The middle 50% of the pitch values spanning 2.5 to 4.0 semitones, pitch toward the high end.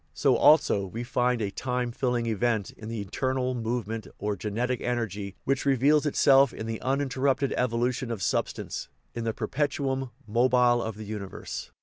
No: average, 2.9 semitones; low, 120 Hz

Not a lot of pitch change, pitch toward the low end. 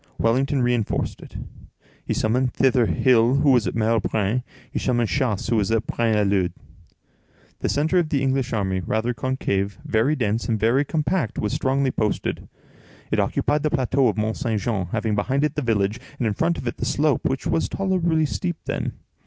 No: average, 4.2 semitones; low, 120 Hz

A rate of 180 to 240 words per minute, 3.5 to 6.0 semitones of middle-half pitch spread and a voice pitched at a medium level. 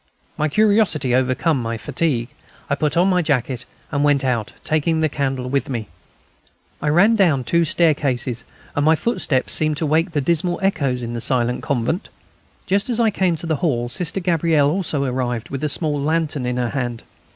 Yes: average, 185 wpm; average, 4.7 semitones; medium, 145 Hz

